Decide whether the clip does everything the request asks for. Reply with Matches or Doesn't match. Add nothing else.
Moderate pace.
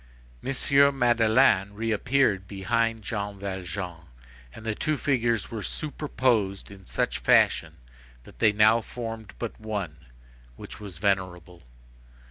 Doesn't match